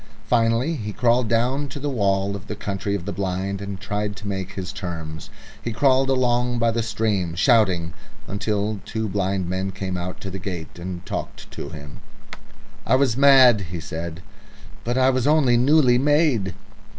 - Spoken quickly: No, average, 175 wpm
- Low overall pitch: Yes, low, 105 Hz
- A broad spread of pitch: No, average, 4.6 semitones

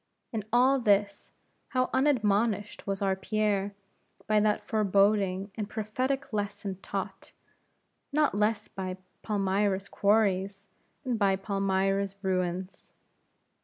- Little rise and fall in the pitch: Yes, narrow, 1.8 semitones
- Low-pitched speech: No, high, 205 Hz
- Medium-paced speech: No, slow, 105 wpm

